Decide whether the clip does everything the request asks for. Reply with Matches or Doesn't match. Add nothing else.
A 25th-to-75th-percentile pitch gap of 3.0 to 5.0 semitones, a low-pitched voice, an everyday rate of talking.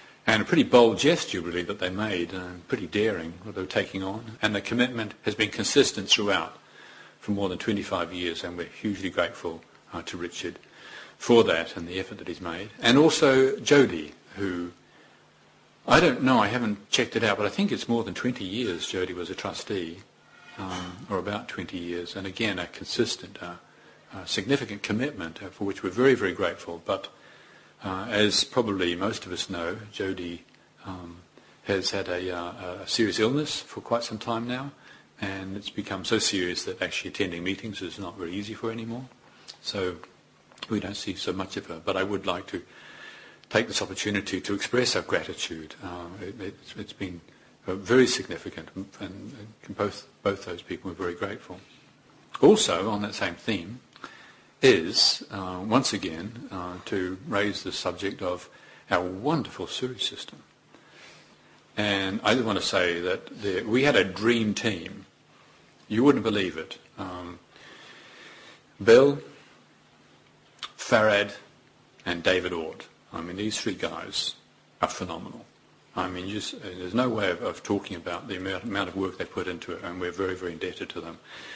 Matches